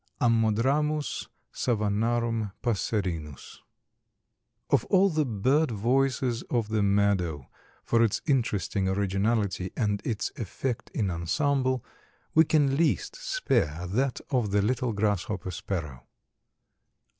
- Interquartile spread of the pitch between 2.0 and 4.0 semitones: No, average, 5.0 semitones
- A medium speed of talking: No, slow, 105 wpm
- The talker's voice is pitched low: Yes, low, 115 Hz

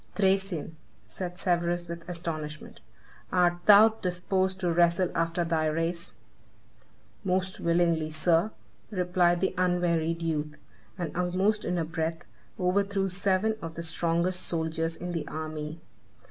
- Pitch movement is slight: Yes, narrow, 1.9 semitones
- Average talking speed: No, slow, 125 wpm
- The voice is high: No, medium, 175 Hz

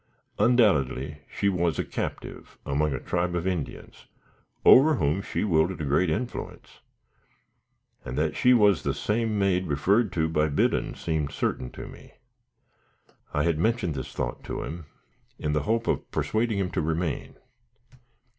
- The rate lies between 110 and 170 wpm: Yes, average, 155 wpm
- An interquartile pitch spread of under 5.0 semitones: No, wide, 5.4 semitones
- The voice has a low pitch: Yes, very low, 85 Hz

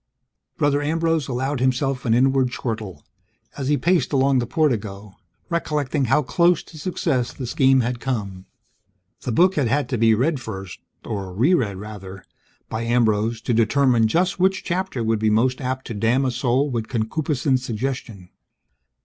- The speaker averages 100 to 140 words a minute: No, average, 165 wpm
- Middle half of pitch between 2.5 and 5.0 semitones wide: Yes, average, 4.4 semitones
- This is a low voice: Yes, low, 125 Hz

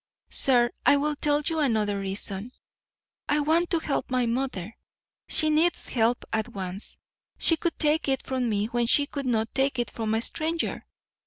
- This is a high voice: Yes, very high, 255 Hz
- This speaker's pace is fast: No, average, 175 wpm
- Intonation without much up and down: No, average, 5.1 semitones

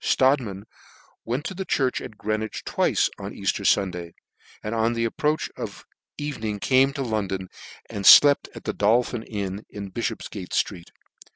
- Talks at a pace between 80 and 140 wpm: No, average, 160 wpm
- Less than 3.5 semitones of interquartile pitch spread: No, average, 4.5 semitones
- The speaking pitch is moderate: No, low, 110 Hz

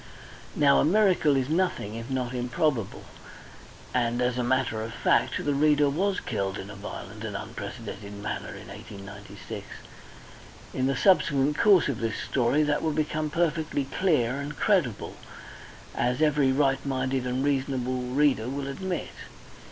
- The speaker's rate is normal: Yes, average, 150 wpm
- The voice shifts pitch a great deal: No, average, 3.6 semitones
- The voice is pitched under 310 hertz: Yes, low, 135 Hz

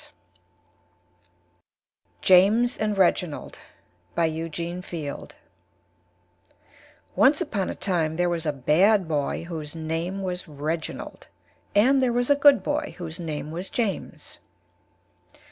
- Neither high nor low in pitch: Yes, medium, 175 Hz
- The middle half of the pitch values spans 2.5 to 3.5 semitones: No, average, 4.3 semitones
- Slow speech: Yes, slow, 115 wpm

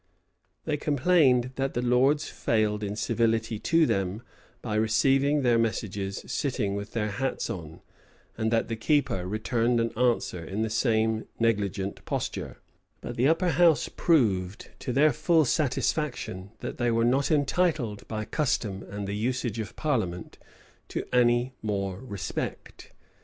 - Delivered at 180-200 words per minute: No, average, 145 wpm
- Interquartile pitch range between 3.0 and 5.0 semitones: Yes, average, 4.4 semitones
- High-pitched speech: No, low, 115 Hz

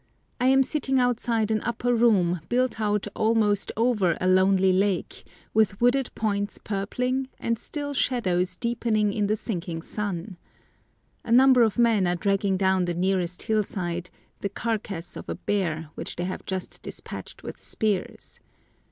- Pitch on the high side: Yes, high, 205 Hz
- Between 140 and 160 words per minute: Yes, average, 150 wpm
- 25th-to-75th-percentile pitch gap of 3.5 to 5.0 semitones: Yes, average, 4.0 semitones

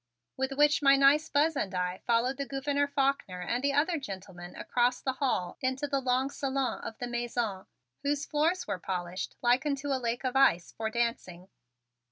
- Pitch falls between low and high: No, very high, 260 Hz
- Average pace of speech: Yes, average, 185 wpm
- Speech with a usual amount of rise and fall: Yes, average, 4.2 semitones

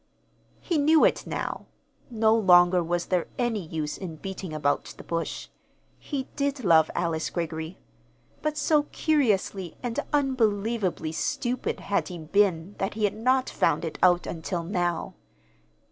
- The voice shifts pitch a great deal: Yes, wide, 6.2 semitones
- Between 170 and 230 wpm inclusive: No, average, 145 wpm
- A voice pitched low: No, high, 190 Hz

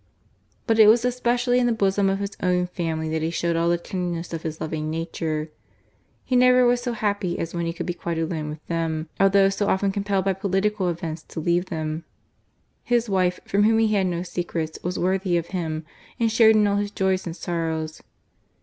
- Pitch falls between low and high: Yes, medium, 180 Hz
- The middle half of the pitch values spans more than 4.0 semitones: No, average, 3.7 semitones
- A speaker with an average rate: No, fast, 210 wpm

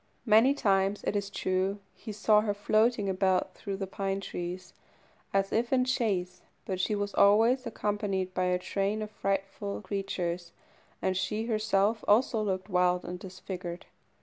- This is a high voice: Yes, high, 195 Hz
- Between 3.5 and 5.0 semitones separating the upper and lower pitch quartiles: No, narrow, 2.4 semitones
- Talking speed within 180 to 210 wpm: No, average, 155 wpm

